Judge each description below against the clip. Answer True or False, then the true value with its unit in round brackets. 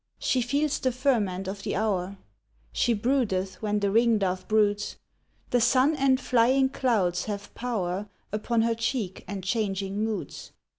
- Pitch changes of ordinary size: True (4.0 semitones)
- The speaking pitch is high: True (215 Hz)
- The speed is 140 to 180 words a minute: True (145 wpm)